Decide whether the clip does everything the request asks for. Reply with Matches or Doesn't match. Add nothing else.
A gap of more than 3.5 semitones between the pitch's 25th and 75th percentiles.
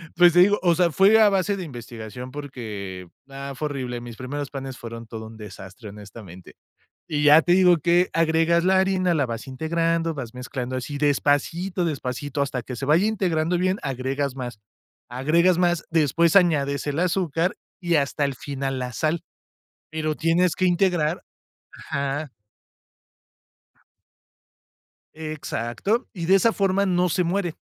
Matches